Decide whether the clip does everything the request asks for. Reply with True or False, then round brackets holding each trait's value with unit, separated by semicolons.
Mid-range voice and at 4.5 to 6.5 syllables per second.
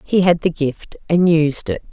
False (160 Hz; 4.2 syllables/s)